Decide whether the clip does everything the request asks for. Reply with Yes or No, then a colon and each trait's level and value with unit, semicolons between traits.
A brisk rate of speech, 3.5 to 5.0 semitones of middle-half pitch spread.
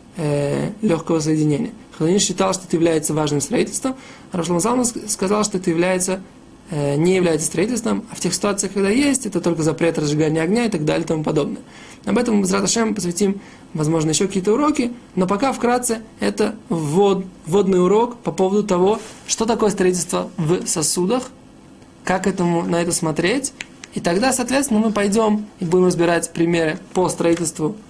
Yes: fast, 165 wpm; average, 4.5 semitones